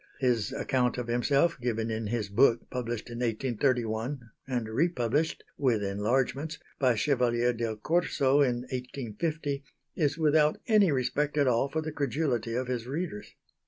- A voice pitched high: No, low, 125 Hz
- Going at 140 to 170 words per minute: Yes, average, 145 wpm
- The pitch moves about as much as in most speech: Yes, average, 3.7 semitones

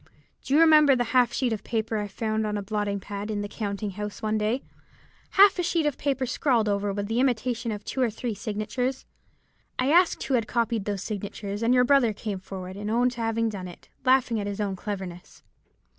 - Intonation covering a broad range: No, average, 3.5 semitones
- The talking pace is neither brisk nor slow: No, fast, 220 wpm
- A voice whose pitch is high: Yes, high, 220 Hz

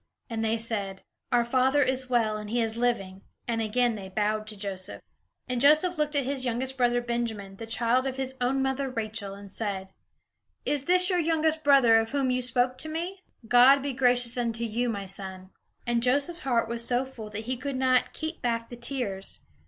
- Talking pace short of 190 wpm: No, average, 200 wpm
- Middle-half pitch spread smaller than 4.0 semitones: Yes, average, 3.3 semitones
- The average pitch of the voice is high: Yes, high, 245 Hz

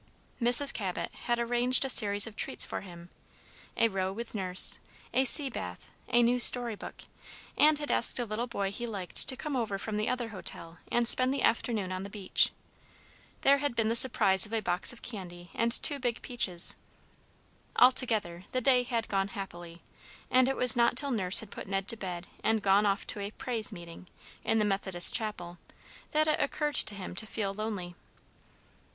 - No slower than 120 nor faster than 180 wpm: No, average, 195 wpm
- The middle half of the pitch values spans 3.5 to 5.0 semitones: Yes, average, 4.1 semitones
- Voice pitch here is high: Yes, high, 220 Hz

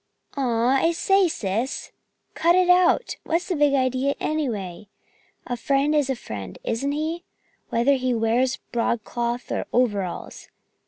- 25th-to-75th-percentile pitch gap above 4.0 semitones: Yes, average, 4.6 semitones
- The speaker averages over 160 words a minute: No, average, 140 wpm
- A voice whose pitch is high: Yes, very high, 260 Hz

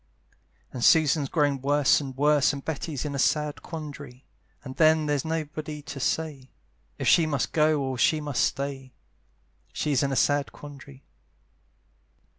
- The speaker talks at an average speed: Yes, average, 150 wpm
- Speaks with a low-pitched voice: No, medium, 145 Hz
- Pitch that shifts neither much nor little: No, narrow, 2.0 semitones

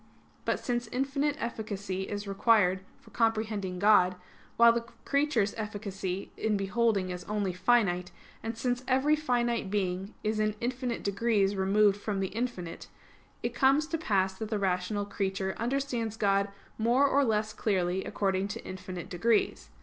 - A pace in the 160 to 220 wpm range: No, average, 150 wpm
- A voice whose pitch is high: Yes, high, 210 Hz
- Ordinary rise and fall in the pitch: Yes, average, 3.5 semitones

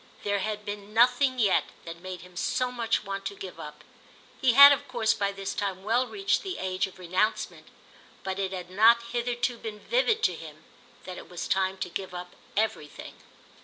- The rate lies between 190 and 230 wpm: Yes, average, 195 wpm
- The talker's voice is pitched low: No, high, 205 Hz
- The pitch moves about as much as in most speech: Yes, average, 4.4 semitones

